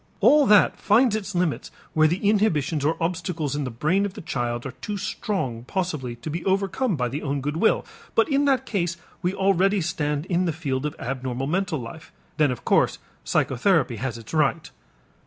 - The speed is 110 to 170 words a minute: No, average, 195 wpm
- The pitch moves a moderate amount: No, wide, 6.1 semitones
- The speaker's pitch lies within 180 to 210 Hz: No, medium, 165 Hz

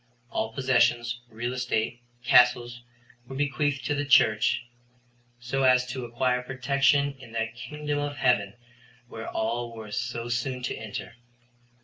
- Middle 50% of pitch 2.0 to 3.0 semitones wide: Yes, narrow, 2.4 semitones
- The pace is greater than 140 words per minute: No, slow, 135 wpm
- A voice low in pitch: Yes, low, 125 Hz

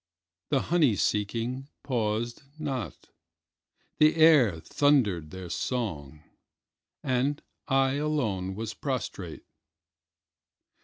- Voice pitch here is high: No, low, 125 Hz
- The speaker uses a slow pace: Yes, slow, 85 wpm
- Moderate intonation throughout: No, wide, 6.1 semitones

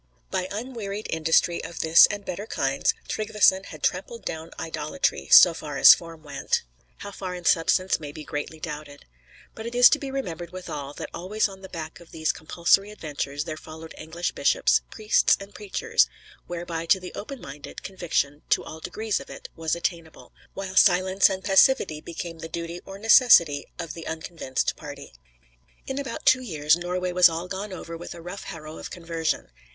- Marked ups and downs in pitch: No, average, 3.6 semitones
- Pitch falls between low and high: Yes, medium, 170 Hz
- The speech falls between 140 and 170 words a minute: No, average, 180 wpm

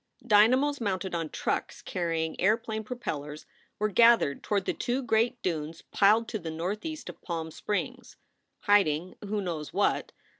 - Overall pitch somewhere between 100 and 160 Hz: No, high, 200 Hz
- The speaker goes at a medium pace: Yes, average, 155 wpm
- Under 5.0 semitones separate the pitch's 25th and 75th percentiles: No, average, 5.3 semitones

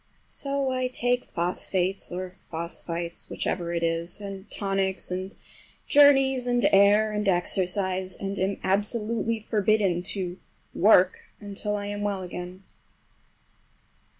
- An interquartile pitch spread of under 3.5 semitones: Yes, average, 2.9 semitones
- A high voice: Yes, high, 195 Hz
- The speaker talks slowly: Yes, slow, 115 wpm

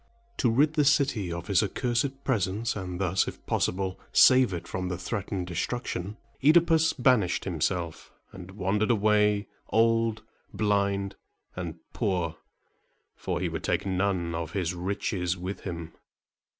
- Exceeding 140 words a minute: No, slow, 135 wpm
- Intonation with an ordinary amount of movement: Yes, average, 4.2 semitones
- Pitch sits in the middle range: No, low, 100 Hz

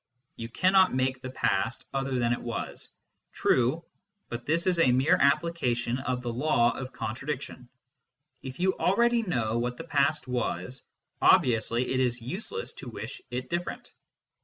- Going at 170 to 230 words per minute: No, average, 160 wpm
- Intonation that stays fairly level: No, average, 4.8 semitones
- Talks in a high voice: No, low, 130 Hz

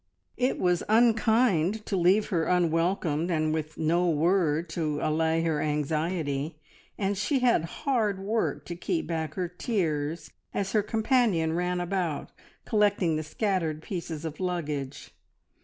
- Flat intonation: No, average, 4.3 semitones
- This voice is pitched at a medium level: Yes, medium, 175 Hz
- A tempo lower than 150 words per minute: Yes, average, 140 wpm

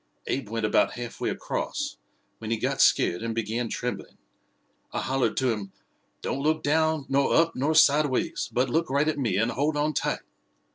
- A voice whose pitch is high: No, low, 130 Hz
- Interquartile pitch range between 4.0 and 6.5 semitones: Yes, average, 4.7 semitones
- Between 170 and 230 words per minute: Yes, average, 185 wpm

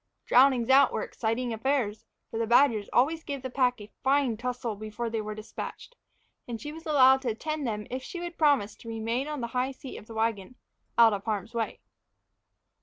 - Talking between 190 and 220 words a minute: Yes, average, 200 wpm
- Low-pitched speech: No, high, 245 Hz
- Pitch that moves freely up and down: No, average, 3.5 semitones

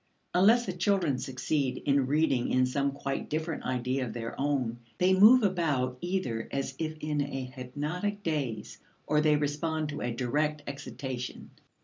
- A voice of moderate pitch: Yes, medium, 145 Hz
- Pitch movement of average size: Yes, average, 3.9 semitones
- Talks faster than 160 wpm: No, average, 155 wpm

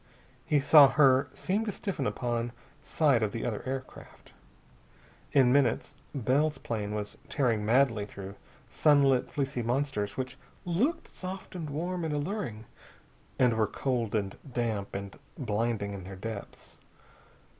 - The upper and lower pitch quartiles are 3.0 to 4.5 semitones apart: No, average, 5.1 semitones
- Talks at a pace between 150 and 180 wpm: No, slow, 135 wpm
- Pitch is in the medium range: No, low, 125 Hz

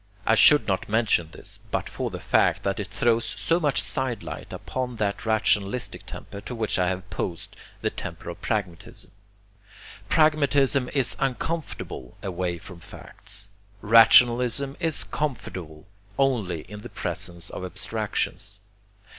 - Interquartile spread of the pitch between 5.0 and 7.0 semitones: Yes, wide, 5.5 semitones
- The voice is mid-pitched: No, low, 110 Hz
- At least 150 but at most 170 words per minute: No, slow, 135 wpm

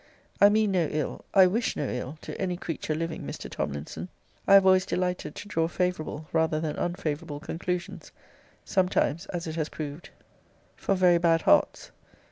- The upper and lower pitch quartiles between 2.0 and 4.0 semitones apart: Yes, average, 3.0 semitones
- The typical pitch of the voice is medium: Yes, medium, 170 Hz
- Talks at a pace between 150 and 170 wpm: Yes, average, 165 wpm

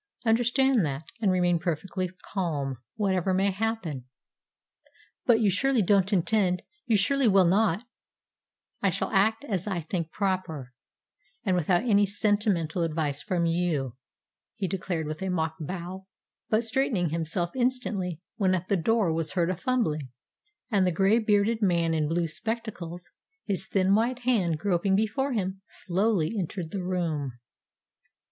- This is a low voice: No, medium, 185 Hz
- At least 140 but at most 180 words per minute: Yes, average, 150 wpm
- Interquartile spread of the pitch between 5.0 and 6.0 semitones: No, average, 4.2 semitones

